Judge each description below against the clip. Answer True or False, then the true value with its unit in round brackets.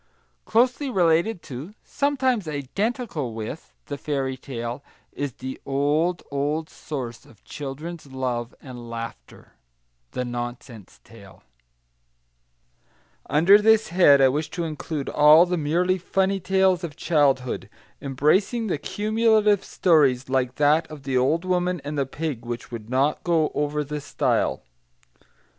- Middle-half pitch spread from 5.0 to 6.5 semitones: True (5.5 semitones)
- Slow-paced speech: True (130 wpm)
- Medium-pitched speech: True (150 Hz)